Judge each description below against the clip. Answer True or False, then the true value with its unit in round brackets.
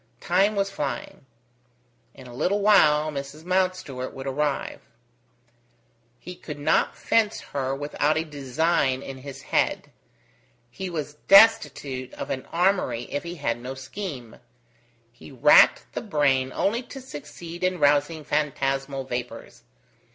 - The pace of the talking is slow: True (130 wpm)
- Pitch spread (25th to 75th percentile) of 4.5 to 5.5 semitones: True (5.0 semitones)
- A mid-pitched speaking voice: True (145 Hz)